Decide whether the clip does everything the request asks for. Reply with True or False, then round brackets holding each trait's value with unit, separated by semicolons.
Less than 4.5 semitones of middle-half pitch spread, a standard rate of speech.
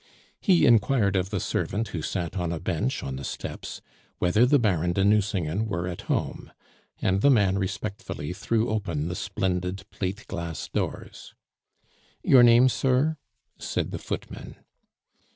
True (4.1 semitones; 150 wpm)